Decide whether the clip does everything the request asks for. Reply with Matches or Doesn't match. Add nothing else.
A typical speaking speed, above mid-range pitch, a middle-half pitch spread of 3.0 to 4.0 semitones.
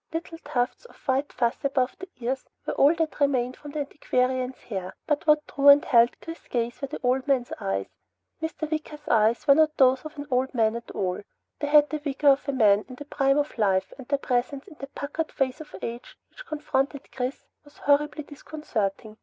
Doesn't match